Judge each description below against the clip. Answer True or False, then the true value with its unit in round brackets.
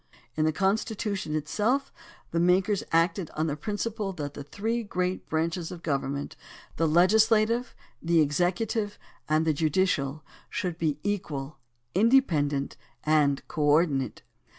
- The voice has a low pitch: False (170 Hz)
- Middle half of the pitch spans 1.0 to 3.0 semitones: False (5.3 semitones)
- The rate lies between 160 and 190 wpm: False (140 wpm)